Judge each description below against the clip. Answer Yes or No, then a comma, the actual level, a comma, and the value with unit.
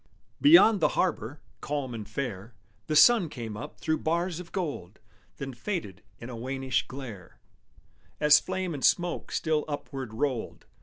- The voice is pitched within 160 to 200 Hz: No, medium, 140 Hz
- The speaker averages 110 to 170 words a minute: Yes, average, 150 wpm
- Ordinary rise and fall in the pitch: No, wide, 6.1 semitones